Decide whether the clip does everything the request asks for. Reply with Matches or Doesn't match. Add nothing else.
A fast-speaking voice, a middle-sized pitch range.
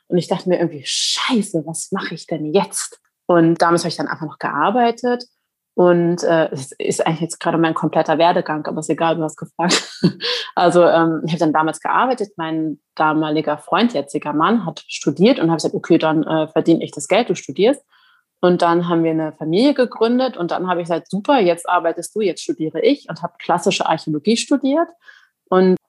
Matches